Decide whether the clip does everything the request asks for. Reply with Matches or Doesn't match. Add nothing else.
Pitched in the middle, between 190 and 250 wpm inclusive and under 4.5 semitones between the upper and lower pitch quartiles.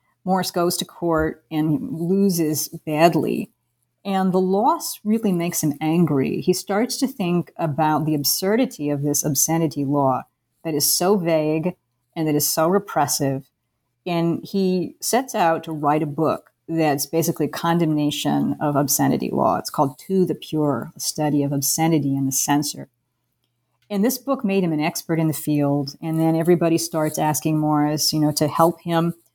Doesn't match